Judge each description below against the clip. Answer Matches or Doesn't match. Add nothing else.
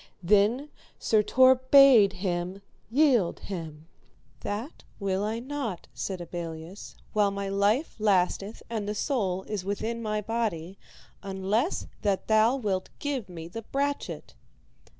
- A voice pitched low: Doesn't match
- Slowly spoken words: Matches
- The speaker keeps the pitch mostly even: Doesn't match